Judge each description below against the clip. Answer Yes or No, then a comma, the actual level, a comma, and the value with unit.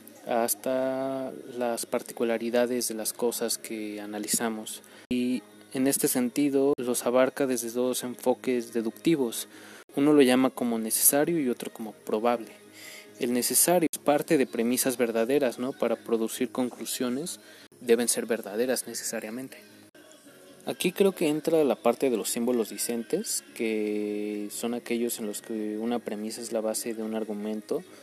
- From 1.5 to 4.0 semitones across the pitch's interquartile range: Yes, average, 2.8 semitones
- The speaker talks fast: No, average, 140 wpm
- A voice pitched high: No, low, 120 Hz